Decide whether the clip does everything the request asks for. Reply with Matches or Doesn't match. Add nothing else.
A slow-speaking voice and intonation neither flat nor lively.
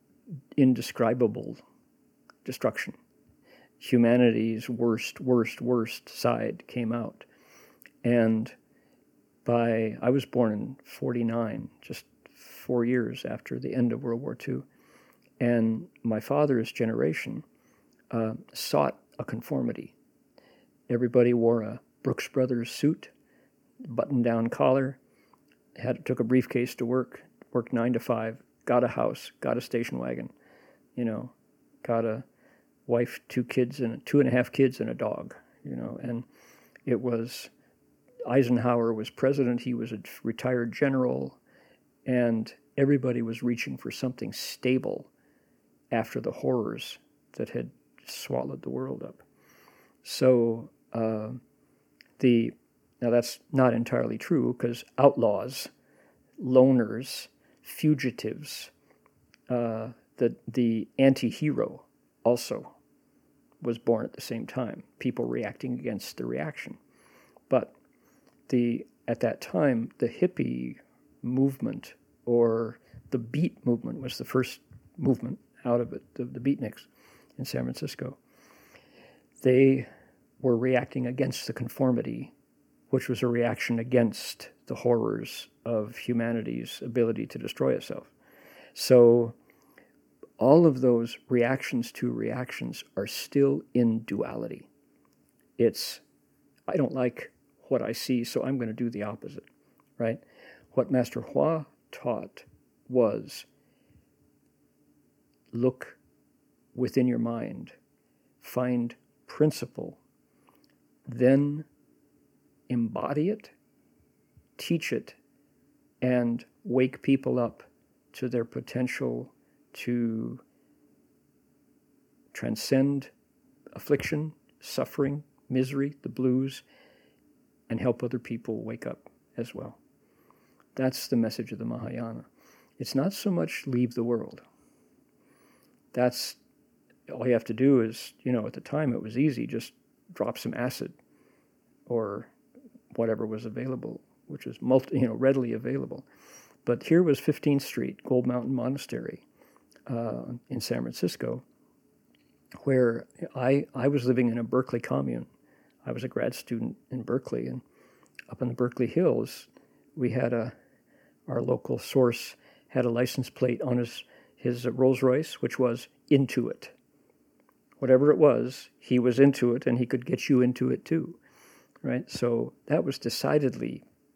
Doesn't match